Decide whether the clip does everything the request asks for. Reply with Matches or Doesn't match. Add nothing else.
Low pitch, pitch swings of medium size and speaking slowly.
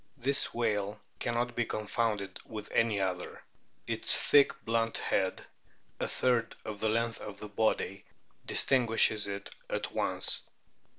Doesn't match